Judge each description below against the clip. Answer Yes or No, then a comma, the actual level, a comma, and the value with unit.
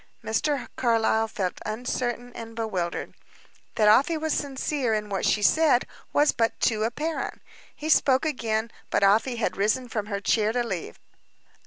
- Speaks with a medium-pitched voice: No, high, 230 Hz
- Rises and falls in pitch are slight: No, average, 3.4 semitones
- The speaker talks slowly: No, average, 155 wpm